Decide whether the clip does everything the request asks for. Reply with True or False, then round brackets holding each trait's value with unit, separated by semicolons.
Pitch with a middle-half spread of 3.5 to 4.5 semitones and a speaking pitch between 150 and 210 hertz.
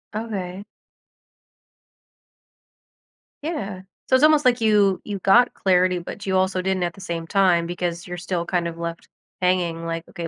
False (2.7 semitones; 185 Hz)